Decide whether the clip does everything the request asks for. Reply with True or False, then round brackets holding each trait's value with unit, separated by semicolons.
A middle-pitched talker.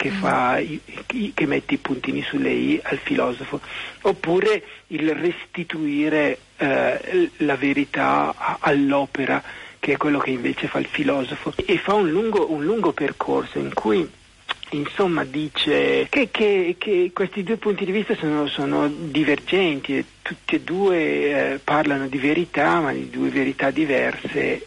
True (155 Hz)